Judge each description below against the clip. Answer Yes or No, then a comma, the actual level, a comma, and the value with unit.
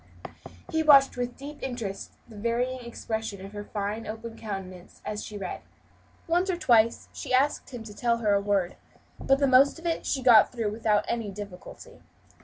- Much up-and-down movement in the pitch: No, average, 3.8 semitones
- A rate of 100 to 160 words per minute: No, average, 185 wpm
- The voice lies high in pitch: Yes, high, 230 Hz